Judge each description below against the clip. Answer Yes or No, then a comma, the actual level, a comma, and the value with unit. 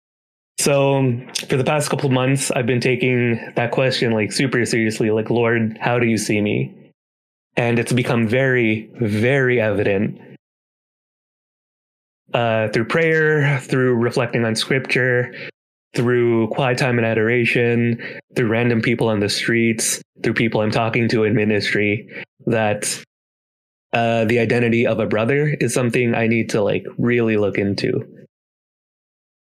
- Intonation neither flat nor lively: No, narrow, 2.3 semitones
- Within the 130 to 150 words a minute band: Yes, average, 140 wpm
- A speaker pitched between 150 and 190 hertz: No, low, 120 Hz